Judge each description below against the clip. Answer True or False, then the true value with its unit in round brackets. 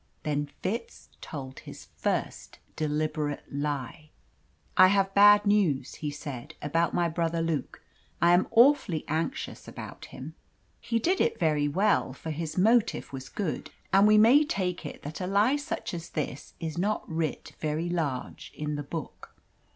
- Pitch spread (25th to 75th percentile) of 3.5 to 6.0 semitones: True (5.1 semitones)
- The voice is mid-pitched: True (165 Hz)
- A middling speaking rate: True (160 wpm)